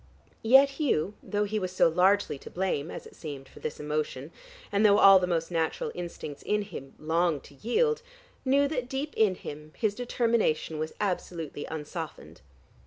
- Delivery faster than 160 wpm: Yes, average, 175 wpm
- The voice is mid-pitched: Yes, medium, 180 Hz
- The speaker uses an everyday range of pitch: No, wide, 5.9 semitones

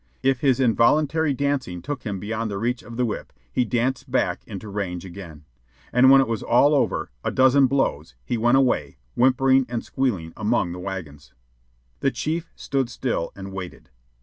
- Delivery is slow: No, average, 175 wpm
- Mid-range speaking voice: No, low, 120 Hz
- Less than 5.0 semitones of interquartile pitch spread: No, wide, 5.5 semitones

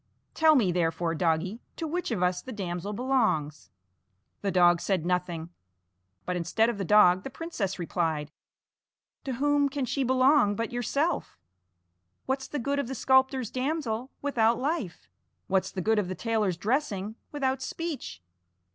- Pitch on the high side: Yes, high, 220 Hz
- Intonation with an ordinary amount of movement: No, wide, 6.8 semitones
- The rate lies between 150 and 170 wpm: Yes, average, 155 wpm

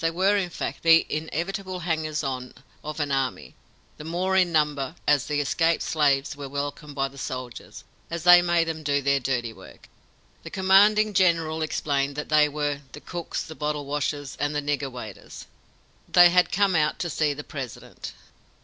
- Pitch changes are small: No, average, 3.2 semitones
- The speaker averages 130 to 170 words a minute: No, average, 180 wpm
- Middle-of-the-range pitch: Yes, medium, 150 Hz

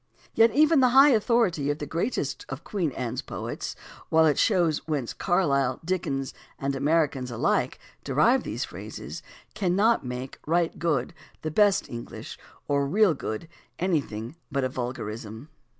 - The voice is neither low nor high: Yes, medium, 155 Hz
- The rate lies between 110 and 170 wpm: Yes, average, 145 wpm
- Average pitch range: No, wide, 6.2 semitones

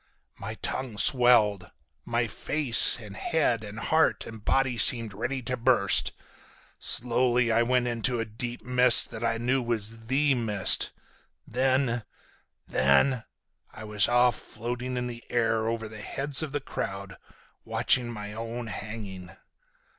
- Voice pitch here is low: Yes, low, 115 Hz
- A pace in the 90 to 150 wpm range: Yes, average, 140 wpm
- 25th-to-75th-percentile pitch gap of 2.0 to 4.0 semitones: Yes, narrow, 2.4 semitones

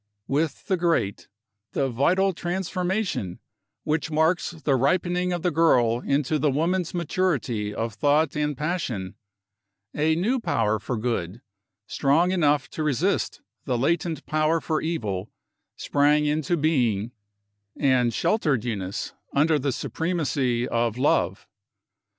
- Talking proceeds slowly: Yes, slow, 125 wpm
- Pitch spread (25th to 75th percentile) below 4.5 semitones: No, wide, 5.4 semitones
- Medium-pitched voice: Yes, medium, 150 Hz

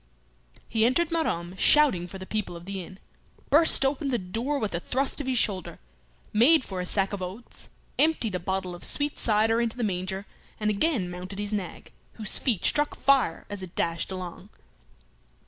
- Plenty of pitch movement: Yes, wide, 6.0 semitones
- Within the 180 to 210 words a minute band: Yes, average, 185 wpm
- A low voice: No, high, 210 Hz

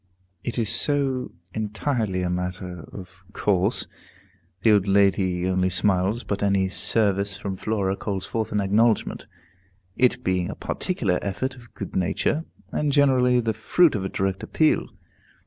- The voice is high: No, low, 100 Hz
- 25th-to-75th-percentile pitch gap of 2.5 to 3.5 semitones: No, average, 4.2 semitones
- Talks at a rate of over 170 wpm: No, average, 145 wpm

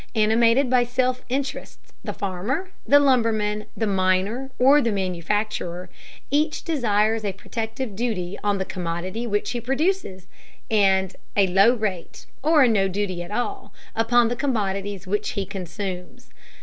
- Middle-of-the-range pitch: No, high, 215 Hz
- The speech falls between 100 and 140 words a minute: Yes, slow, 135 wpm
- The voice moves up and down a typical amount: Yes, average, 4.3 semitones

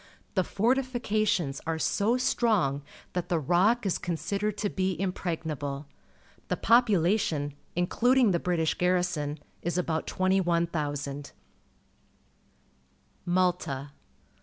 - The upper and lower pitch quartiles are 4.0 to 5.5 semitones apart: Yes, average, 4.5 semitones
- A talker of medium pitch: Yes, medium, 180 Hz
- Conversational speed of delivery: No, slow, 95 wpm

